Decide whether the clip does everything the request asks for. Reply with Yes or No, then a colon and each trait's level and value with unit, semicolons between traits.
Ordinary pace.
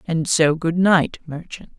Yes: average, 170 wpm